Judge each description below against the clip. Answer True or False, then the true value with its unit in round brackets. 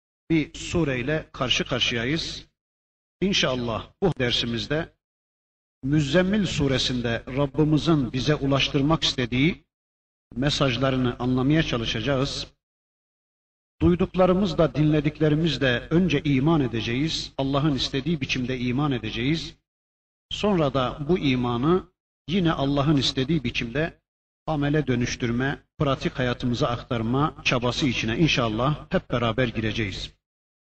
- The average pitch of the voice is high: False (135 Hz)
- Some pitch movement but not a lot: True (4.3 semitones)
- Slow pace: True (90 wpm)